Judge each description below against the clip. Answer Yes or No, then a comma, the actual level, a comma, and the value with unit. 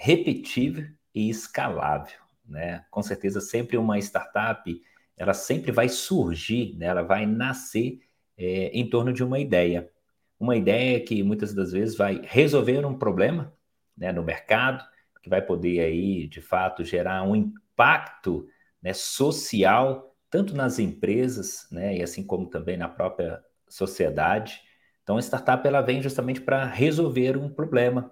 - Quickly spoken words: No, average, 145 wpm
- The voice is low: Yes, low, 120 Hz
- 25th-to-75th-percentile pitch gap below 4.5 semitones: No, wide, 5.6 semitones